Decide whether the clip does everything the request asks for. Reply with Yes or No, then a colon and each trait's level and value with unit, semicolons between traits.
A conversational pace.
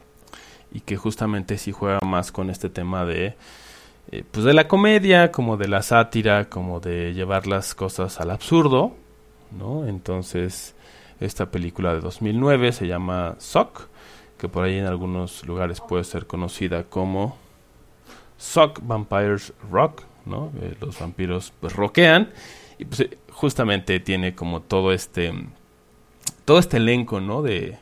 Yes: average, 145 wpm